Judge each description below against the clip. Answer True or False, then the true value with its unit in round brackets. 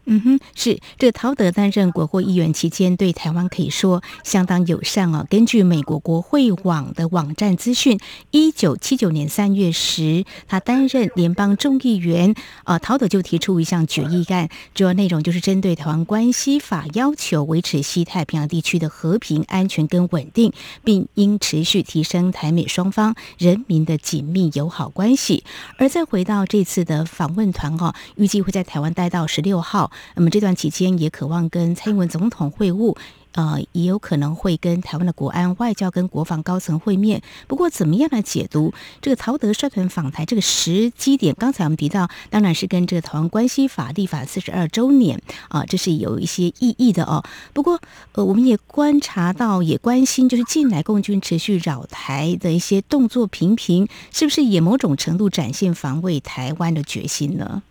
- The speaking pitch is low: False (185 Hz)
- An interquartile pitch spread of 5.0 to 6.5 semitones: False (4.3 semitones)